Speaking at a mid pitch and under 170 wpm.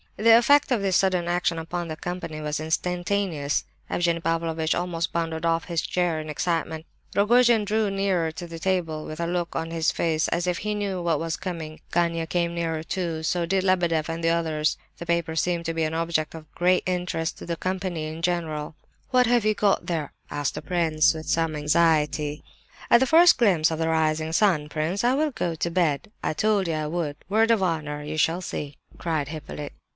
No: medium, 170 Hz; average, 200 wpm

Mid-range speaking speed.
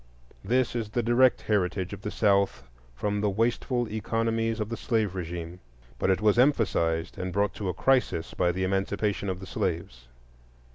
Yes: average, 175 wpm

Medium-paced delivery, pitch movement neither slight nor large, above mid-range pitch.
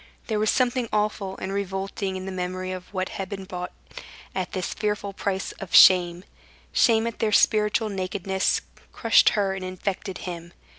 No: average, 165 wpm; narrow, 2.2 semitones; high, 195 Hz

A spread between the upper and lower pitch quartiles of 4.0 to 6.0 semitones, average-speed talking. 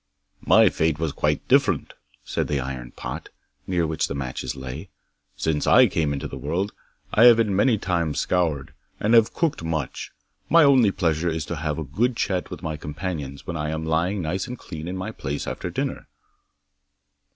Yes: average, 4.3 semitones; average, 185 wpm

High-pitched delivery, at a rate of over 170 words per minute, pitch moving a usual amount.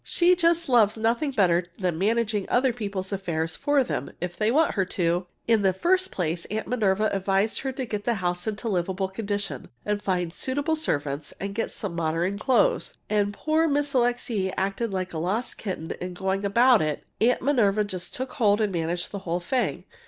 Yes: high, 205 Hz; average, 190 wpm; average, 4.9 semitones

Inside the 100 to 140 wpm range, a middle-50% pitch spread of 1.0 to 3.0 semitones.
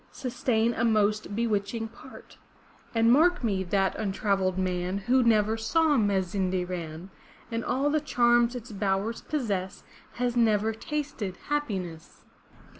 No: slow, 135 wpm; average, 3.8 semitones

